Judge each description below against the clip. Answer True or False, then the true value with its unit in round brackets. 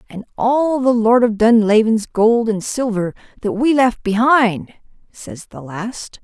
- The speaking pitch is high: True (225 Hz)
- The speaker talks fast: False (155 wpm)